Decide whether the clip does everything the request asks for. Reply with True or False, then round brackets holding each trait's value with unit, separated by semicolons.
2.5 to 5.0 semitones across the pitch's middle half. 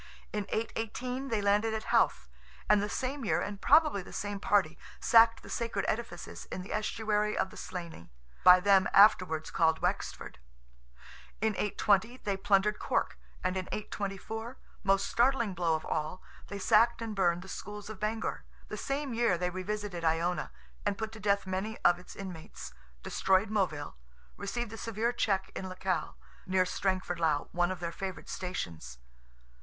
True (3.2 semitones)